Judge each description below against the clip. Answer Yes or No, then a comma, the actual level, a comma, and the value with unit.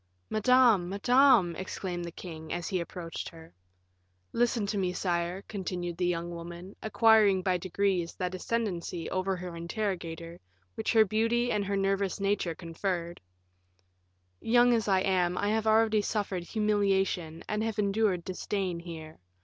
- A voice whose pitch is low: No, high, 190 Hz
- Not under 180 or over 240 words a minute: No, average, 145 wpm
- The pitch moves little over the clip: No, average, 3.5 semitones